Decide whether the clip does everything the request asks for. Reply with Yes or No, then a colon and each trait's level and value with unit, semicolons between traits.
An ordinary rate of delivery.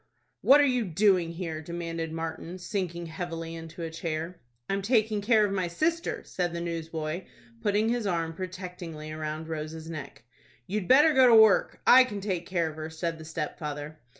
Yes: average, 180 wpm